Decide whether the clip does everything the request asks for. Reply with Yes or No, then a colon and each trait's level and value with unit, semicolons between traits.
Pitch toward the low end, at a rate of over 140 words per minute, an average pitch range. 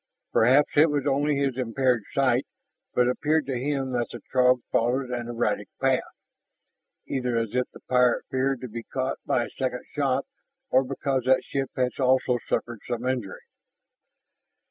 No: low, 130 Hz; average, 165 wpm; narrow, 1.8 semitones